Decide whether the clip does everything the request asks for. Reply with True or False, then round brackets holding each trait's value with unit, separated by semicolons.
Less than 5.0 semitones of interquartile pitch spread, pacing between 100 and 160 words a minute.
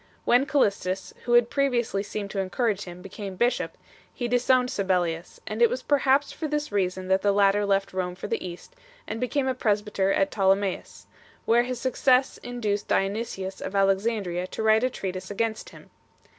False (4.1 semitones; 180 wpm)